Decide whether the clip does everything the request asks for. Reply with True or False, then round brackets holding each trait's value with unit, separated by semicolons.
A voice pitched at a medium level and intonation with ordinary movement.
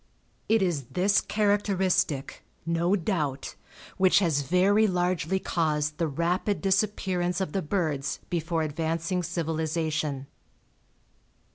True (170 Hz; 3.4 semitones)